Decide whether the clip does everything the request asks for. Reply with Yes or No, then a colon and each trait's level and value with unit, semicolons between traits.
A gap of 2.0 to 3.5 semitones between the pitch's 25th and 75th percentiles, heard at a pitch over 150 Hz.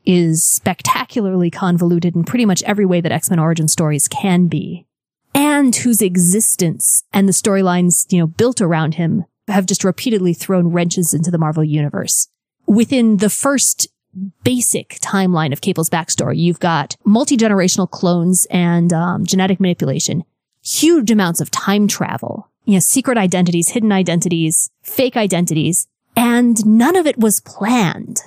No: average, 4.1 semitones; medium, 185 Hz